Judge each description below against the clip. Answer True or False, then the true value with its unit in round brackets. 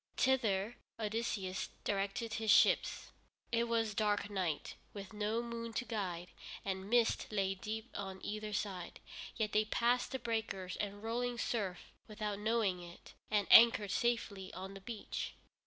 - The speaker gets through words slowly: False (145 wpm)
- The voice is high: True (210 Hz)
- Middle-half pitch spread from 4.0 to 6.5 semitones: False (2.9 semitones)